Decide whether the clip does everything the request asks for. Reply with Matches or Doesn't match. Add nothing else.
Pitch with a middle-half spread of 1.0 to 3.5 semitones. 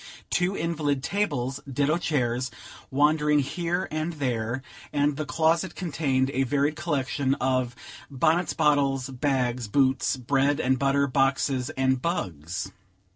Matches